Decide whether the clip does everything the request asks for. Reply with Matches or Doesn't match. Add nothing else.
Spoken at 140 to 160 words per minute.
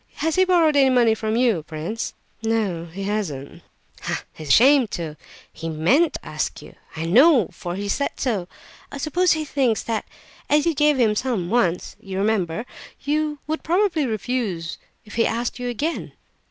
Doesn't match